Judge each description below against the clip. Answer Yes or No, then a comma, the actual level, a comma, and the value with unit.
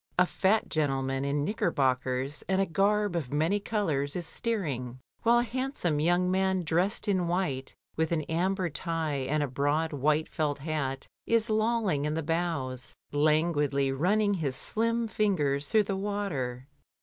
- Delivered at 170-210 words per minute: No, average, 155 wpm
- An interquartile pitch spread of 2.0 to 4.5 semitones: No, wide, 5.6 semitones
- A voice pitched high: No, medium, 160 Hz